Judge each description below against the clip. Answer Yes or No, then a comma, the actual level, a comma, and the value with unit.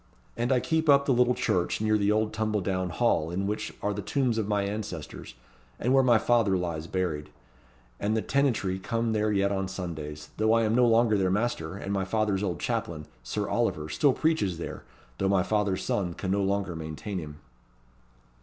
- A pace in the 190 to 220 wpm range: Yes, average, 200 wpm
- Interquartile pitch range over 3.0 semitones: Yes, average, 3.5 semitones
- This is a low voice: Yes, low, 100 Hz